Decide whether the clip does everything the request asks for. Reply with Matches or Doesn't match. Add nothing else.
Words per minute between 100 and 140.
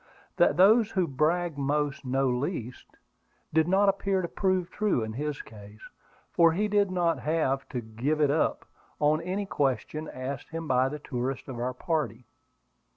Doesn't match